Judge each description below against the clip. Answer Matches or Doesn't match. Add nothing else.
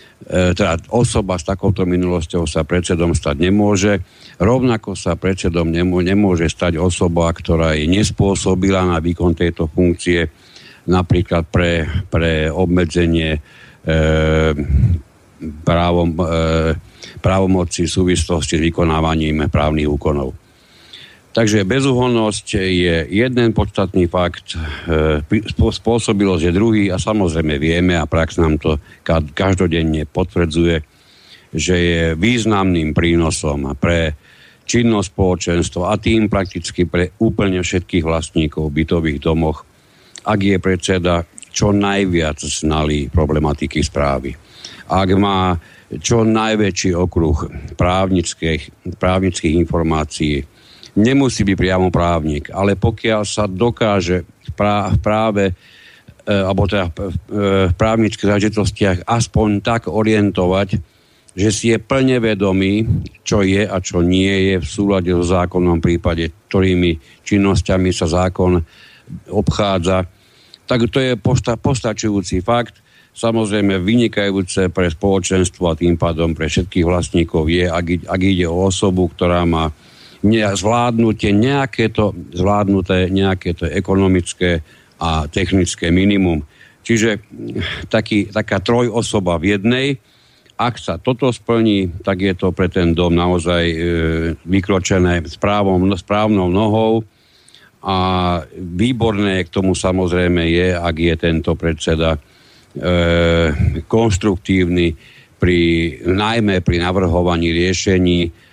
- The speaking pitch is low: Matches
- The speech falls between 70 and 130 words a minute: Matches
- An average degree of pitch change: Matches